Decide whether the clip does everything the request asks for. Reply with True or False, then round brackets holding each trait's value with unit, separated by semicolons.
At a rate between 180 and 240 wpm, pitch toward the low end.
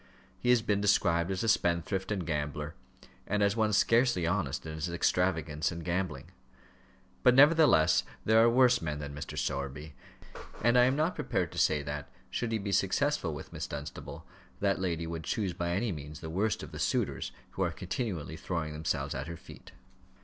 True (185 wpm; 90 Hz)